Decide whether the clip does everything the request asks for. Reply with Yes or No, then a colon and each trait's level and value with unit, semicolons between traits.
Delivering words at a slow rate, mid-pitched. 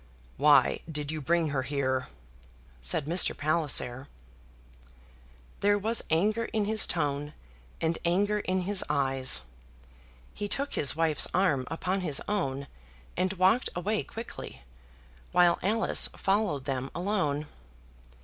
Yes: slow, 120 wpm; medium, 165 Hz